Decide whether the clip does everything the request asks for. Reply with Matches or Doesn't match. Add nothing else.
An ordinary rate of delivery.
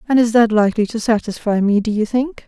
Doesn't match